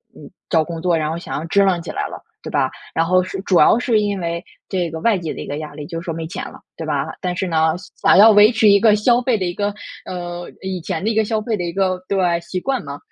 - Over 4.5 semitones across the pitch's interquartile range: No, average, 3.5 semitones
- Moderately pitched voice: Yes, medium, 180 Hz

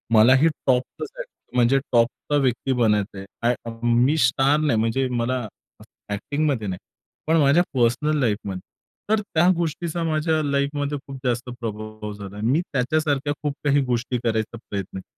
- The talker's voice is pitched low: Yes, low, 130 Hz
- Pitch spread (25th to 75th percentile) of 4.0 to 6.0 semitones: Yes, average, 4.4 semitones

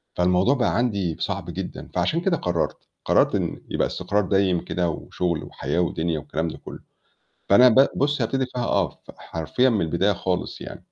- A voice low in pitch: Yes, very low, 95 Hz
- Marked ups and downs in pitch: Yes, wide, 6.3 semitones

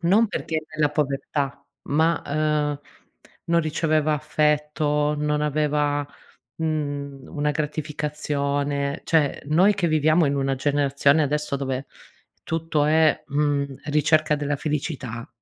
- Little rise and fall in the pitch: Yes, narrow, 1.4 semitones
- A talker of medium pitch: Yes, medium, 150 Hz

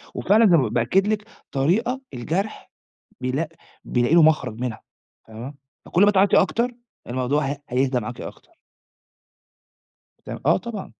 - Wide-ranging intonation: Yes, wide, 7.9 semitones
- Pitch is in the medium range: Yes, medium, 145 Hz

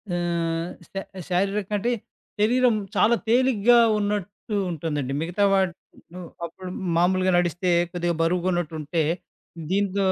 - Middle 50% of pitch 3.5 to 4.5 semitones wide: No, average, 3.1 semitones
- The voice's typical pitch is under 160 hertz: No, medium, 185 Hz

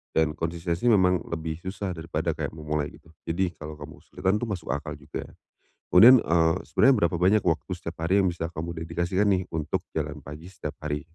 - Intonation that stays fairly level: No, average, 3.0 semitones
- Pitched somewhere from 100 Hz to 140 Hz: No, very low, 85 Hz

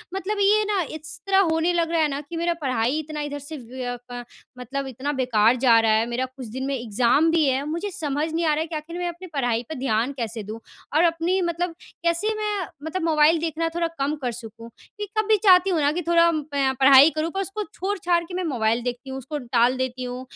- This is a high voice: Yes, very high, 300 Hz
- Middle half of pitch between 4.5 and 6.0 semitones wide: Yes, average, 5.1 semitones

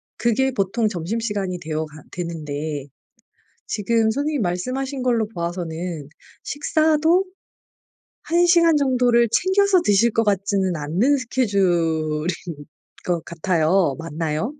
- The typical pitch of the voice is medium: No, high, 200 Hz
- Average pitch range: No, wide, 7.5 semitones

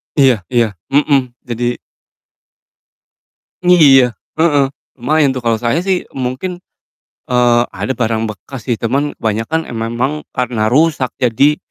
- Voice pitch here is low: Yes, low, 125 Hz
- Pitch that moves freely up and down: No, average, 3.6 semitones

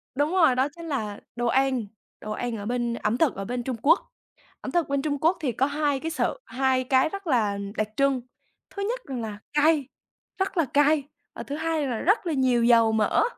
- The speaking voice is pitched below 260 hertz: No, very high, 270 Hz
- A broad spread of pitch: No, average, 4.5 semitones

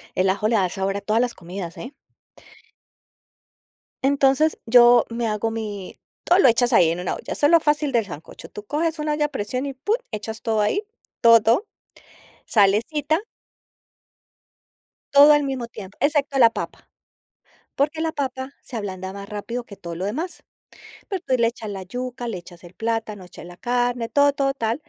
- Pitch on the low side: No, high, 235 Hz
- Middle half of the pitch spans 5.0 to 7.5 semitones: Yes, wide, 5.5 semitones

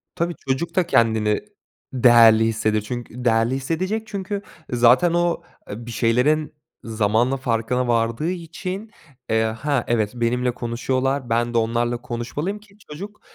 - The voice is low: Yes, low, 125 Hz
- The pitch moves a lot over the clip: Yes, wide, 6.1 semitones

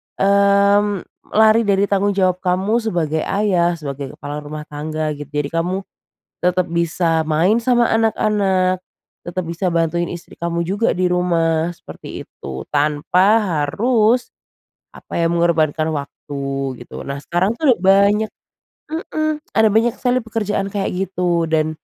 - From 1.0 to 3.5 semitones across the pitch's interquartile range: No, average, 4.2 semitones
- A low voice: No, medium, 180 Hz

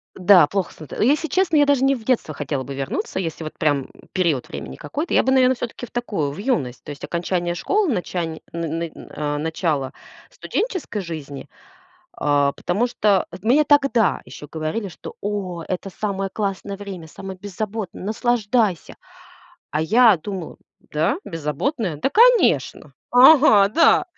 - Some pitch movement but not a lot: No, wide, 7.3 semitones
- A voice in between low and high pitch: No, high, 195 Hz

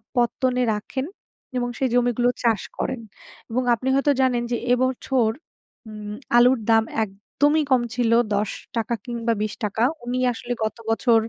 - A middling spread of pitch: No, narrow, 2.2 semitones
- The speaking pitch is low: No, high, 240 Hz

